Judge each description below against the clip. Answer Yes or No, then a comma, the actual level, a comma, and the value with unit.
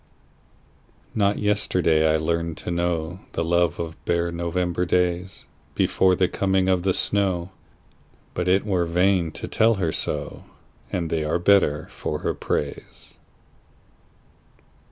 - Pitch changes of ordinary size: No, narrow, 2.1 semitones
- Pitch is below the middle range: Yes, very low, 85 Hz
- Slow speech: Yes, slow, 115 wpm